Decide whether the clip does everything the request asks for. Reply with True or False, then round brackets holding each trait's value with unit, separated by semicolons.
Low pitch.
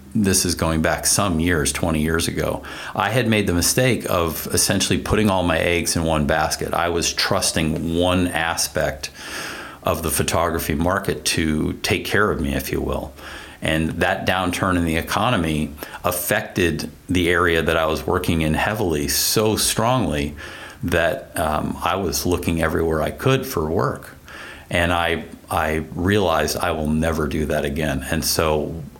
True (85 Hz)